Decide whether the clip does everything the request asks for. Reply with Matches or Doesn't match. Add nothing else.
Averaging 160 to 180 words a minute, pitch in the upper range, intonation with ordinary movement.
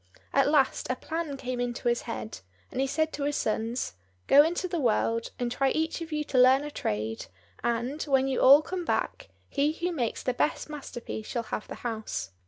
Doesn't match